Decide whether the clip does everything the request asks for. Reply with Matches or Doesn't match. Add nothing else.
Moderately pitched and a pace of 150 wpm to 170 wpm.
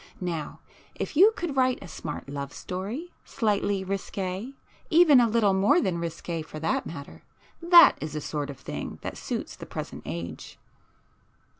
Doesn't match